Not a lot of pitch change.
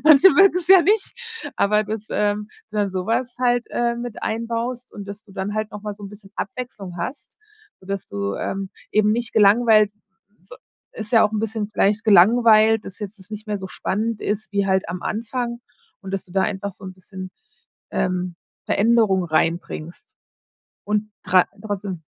No: average, 3.0 semitones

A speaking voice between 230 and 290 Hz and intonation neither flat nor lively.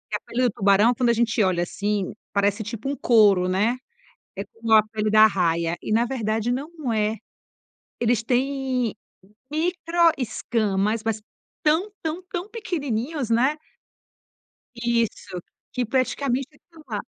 Yes: high, 235 Hz; average, 4.3 semitones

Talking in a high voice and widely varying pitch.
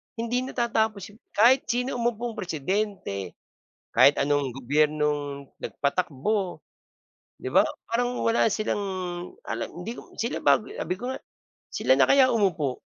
Yes: high, 205 Hz; wide, 8.3 semitones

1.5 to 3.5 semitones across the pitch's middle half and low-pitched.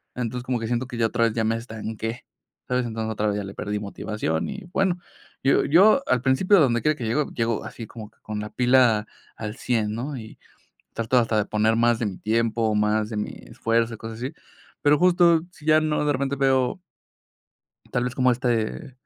Yes: average, 3.2 semitones; low, 115 Hz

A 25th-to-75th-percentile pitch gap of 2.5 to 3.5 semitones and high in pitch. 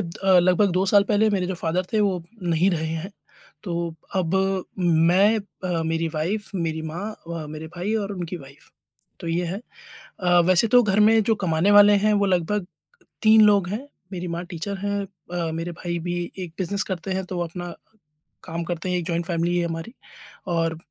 No: average, 3.0 semitones; medium, 180 Hz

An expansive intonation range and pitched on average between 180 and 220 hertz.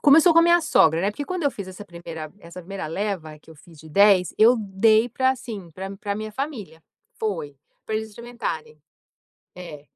Yes: wide, 5.9 semitones; high, 200 Hz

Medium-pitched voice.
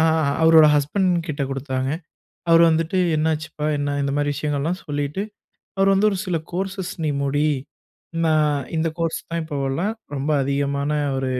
Yes: medium, 150 Hz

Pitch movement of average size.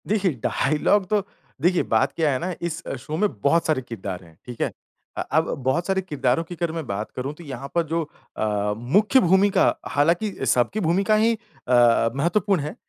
No: wide, 7.0 semitones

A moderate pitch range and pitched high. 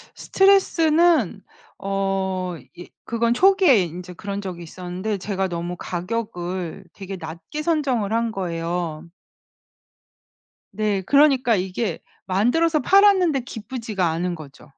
No: wide, 6.3 semitones; high, 195 Hz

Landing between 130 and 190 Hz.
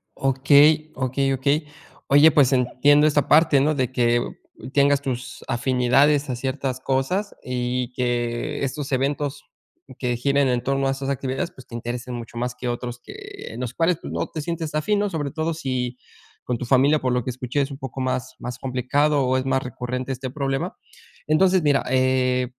Yes: low, 135 Hz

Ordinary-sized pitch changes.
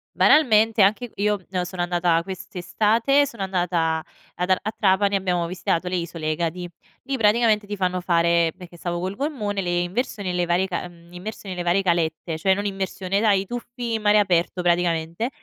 Yes: average, 3.1 semitones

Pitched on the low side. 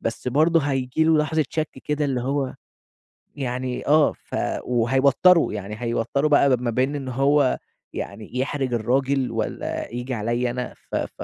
Yes: low, 130 Hz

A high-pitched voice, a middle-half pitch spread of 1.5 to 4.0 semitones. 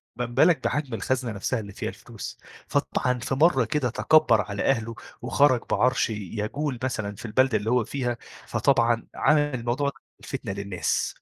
No: low, 120 Hz; average, 3.5 semitones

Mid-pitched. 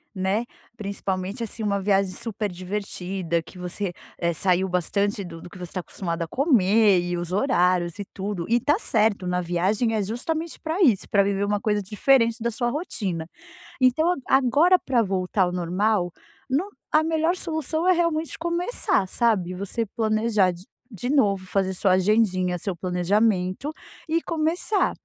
No: high, 205 Hz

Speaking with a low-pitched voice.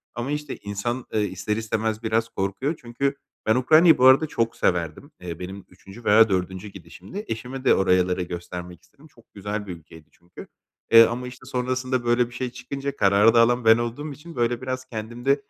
Yes: low, 115 Hz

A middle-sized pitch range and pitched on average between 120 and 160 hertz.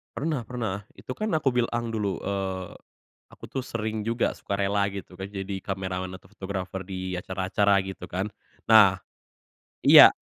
No: average, 3.2 semitones; low, 100 Hz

